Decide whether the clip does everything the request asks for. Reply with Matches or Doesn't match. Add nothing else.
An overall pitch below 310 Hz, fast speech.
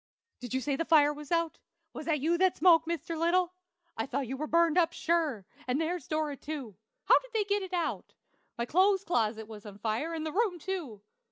Doesn't match